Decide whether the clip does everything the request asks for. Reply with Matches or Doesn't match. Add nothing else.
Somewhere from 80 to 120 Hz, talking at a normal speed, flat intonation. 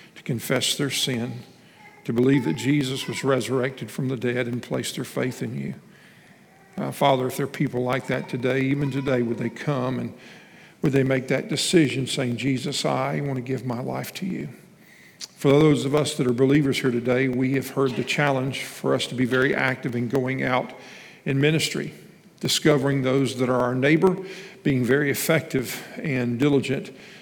Doesn't match